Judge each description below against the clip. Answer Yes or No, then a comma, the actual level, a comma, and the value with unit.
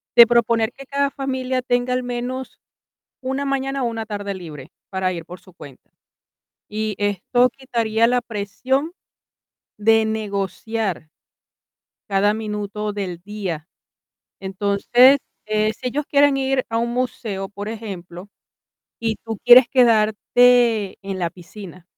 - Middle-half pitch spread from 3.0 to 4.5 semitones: Yes, average, 3.8 semitones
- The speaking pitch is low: No, high, 220 Hz